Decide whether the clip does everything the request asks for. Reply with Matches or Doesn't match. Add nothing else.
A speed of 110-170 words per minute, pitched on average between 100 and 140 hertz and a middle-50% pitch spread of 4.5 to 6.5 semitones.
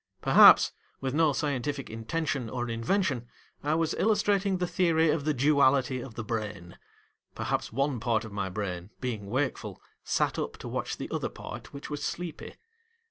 Matches